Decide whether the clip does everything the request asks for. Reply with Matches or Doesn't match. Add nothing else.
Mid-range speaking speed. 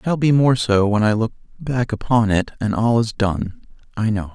Doesn't match